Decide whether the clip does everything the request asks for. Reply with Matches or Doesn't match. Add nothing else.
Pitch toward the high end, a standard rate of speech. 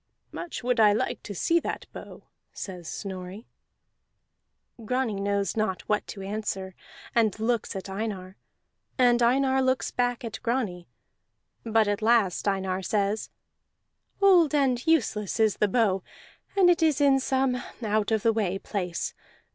Matches